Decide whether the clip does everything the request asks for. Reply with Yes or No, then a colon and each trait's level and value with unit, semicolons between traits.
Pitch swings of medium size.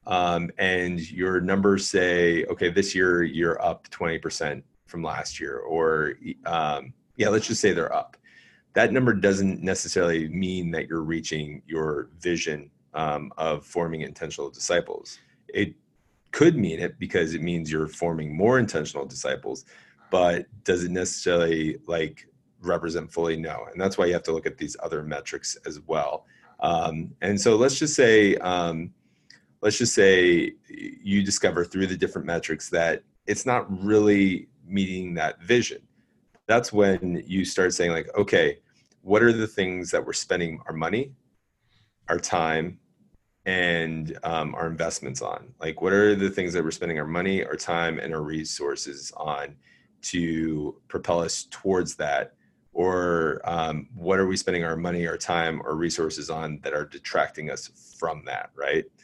Yes: average, 3.3 semitones